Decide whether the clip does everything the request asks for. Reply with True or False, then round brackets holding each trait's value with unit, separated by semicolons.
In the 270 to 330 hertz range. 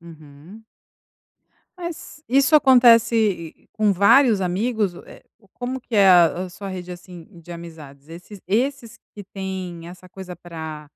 False (190 Hz)